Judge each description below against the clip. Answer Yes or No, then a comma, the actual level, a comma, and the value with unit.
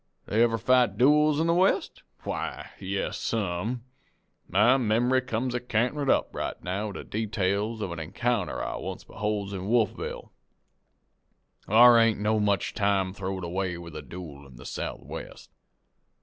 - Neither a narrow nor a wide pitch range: Yes, average, 4.3 semitones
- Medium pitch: No, low, 110 Hz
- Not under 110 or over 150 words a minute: No, average, 160 wpm